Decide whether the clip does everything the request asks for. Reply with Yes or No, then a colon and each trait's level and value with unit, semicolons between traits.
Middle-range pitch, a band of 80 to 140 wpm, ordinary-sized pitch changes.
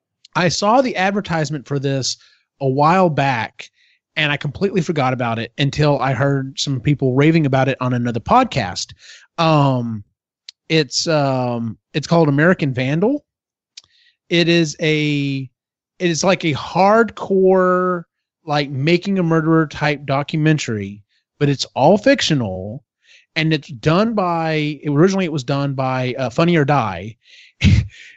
Yes: medium, 150 Hz; slow, 135 wpm; average, 4.3 semitones